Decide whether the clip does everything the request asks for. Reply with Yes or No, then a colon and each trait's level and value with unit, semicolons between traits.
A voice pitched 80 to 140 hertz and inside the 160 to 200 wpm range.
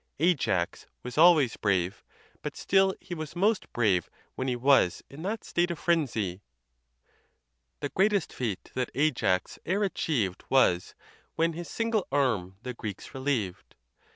No: low, 135 Hz; average, 140 wpm